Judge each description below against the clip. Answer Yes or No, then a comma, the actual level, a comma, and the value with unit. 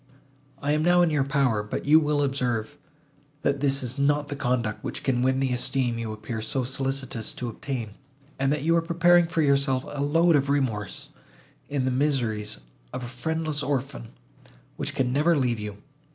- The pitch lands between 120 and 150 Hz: Yes, low, 135 Hz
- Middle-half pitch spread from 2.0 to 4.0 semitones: Yes, average, 3.1 semitones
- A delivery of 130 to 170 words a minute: No, average, 185 wpm